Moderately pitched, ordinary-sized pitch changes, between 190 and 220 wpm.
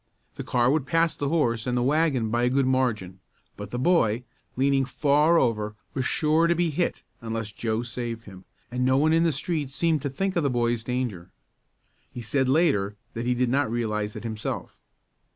No: low, 125 Hz; average, 4.5 semitones; average, 200 wpm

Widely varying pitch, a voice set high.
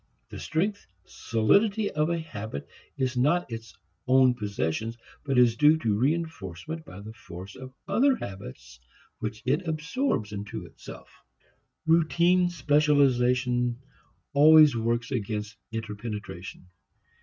No: wide, 6.7 semitones; low, 125 Hz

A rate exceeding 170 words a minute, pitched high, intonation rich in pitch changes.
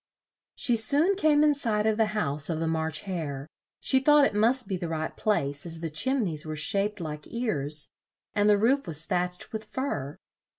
Yes: average, 200 wpm; high, 195 Hz; wide, 6.9 semitones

